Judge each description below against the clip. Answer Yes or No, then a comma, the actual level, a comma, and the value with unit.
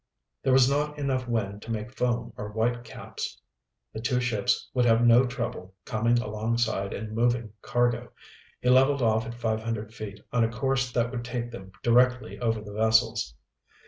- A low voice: Yes, low, 120 Hz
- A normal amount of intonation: No, narrow, 1.8 semitones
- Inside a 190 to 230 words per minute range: No, average, 175 wpm